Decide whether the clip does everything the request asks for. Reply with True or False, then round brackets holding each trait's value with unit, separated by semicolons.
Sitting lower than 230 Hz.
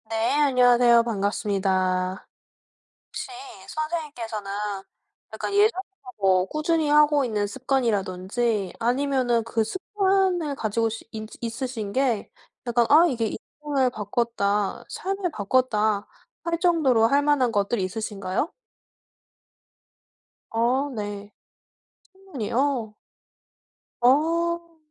False (240 Hz)